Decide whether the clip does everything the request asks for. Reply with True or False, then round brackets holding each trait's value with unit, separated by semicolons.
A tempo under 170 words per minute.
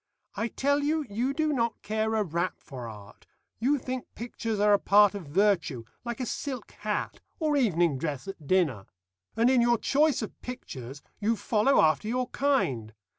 False (175 wpm)